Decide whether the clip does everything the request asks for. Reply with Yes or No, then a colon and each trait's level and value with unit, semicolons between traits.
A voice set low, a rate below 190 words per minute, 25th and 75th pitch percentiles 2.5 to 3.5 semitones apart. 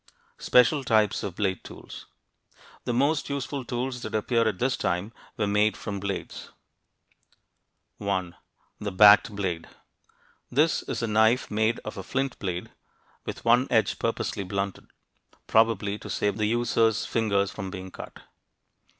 Yes: low, 110 Hz; average, 140 wpm; average, 3.1 semitones